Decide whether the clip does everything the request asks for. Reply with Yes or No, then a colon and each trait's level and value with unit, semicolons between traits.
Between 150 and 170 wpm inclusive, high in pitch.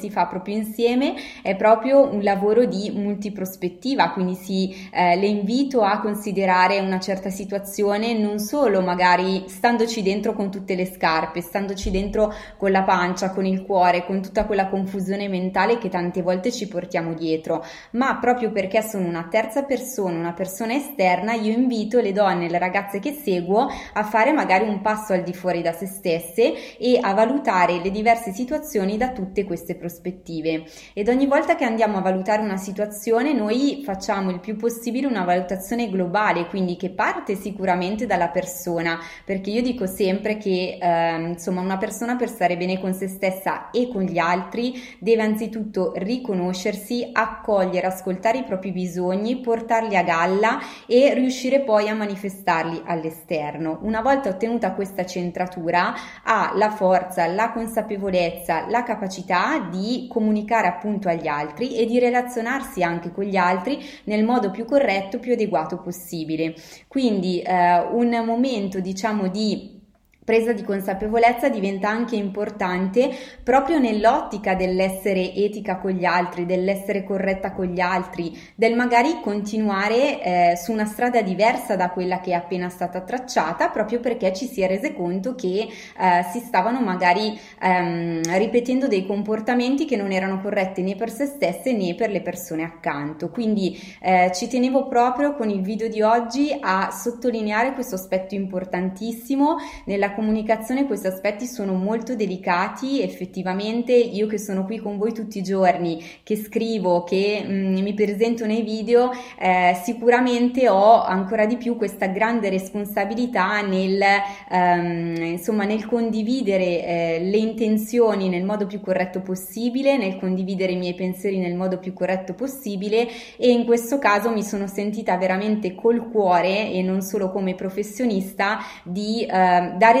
Yes: average, 155 wpm; high, 200 Hz